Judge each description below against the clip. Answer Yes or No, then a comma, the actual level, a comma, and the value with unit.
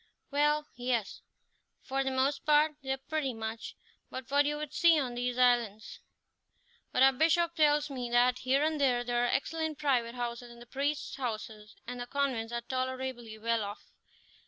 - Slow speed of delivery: No, average, 175 wpm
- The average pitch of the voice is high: Yes, very high, 260 Hz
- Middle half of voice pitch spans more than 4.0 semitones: No, average, 3.2 semitones